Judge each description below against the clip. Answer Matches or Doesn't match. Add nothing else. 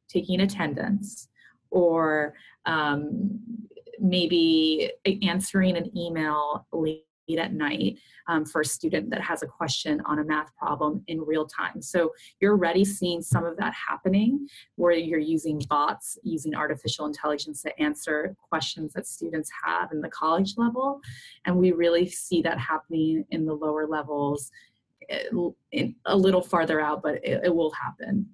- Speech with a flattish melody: Doesn't match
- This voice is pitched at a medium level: Matches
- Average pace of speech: Matches